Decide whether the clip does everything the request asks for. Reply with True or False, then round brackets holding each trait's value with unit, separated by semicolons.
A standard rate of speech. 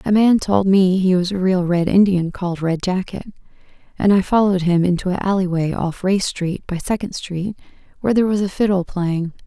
False (210 wpm)